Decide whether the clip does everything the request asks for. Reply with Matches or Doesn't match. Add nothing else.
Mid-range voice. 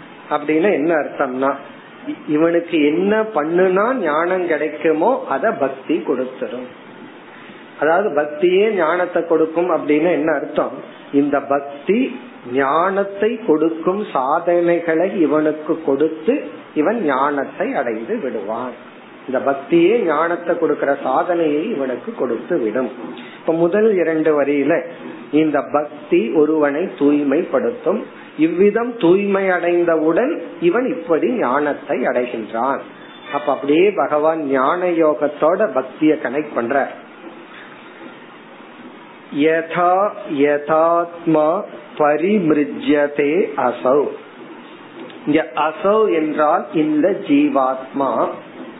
Matches